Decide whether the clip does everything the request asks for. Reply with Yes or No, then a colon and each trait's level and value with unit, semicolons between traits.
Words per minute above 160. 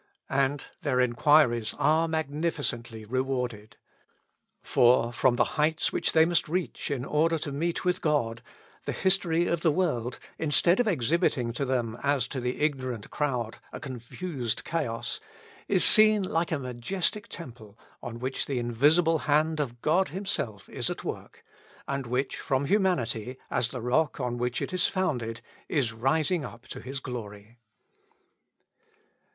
No: average, 150 wpm